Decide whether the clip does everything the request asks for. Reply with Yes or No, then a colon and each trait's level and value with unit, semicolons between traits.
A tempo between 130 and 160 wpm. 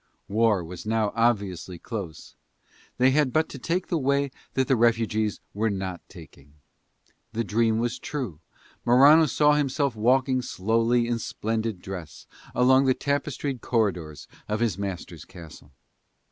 Yes: average, 140 wpm